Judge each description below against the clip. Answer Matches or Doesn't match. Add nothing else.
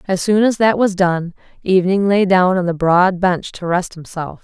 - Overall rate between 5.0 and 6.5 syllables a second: Doesn't match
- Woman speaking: Matches